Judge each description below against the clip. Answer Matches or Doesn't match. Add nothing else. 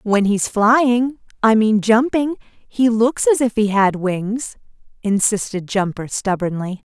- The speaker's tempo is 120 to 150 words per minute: Matches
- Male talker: Doesn't match